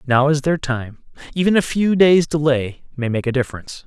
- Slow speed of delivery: No, average, 200 wpm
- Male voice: Yes, male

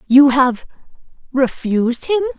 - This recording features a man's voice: No, female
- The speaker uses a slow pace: Yes, slow, 75 wpm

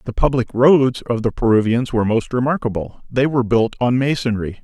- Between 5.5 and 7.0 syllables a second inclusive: Yes, 5.6 syllables/s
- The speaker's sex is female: No, male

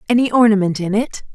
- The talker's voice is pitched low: No, high, 215 Hz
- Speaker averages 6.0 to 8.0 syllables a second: Yes, 6.4 syllables/s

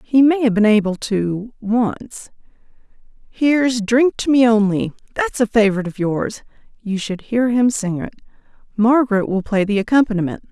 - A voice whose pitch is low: No, high, 220 Hz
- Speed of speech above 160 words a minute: No, average, 155 wpm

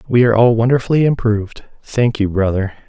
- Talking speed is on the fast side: No, average, 165 wpm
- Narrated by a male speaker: Yes, male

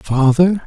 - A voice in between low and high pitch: Yes, medium, 155 Hz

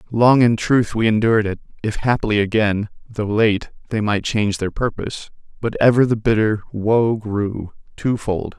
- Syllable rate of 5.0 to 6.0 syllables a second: No, 4.6 syllables/s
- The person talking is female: No, male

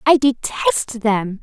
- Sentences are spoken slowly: Yes, slow, 125 wpm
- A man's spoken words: No, female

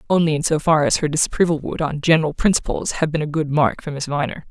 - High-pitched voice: No, medium, 155 Hz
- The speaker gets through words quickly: Yes, fast, 255 wpm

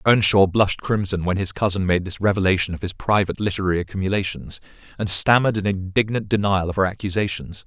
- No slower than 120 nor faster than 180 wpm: Yes, average, 170 wpm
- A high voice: No, very low, 95 Hz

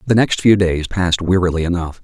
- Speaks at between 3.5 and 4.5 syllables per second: No, 6.0 syllables/s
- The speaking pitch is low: Yes, very low, 90 Hz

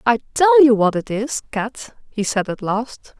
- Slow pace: No, fast, 205 wpm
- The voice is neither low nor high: No, high, 235 Hz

